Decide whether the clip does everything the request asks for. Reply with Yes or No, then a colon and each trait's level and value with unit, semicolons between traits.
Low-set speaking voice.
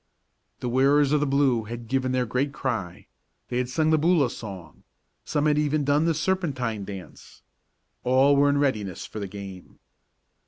Yes: low, 130 Hz